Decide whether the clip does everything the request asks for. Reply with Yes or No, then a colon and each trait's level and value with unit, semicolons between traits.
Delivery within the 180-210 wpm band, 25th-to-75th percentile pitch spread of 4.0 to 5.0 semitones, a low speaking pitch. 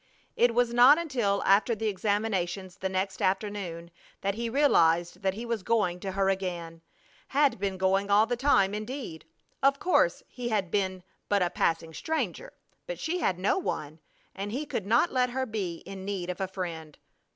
No: average, 185 wpm; average, 4.3 semitones; high, 200 Hz